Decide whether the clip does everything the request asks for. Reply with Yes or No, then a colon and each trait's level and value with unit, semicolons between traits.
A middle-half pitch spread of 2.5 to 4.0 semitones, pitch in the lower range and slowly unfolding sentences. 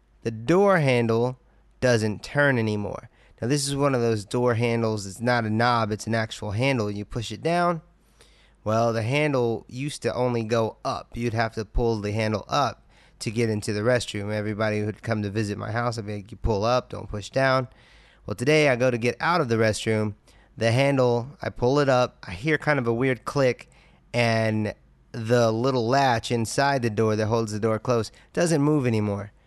No: average, 2.8 semitones; low, 115 Hz; fast, 205 wpm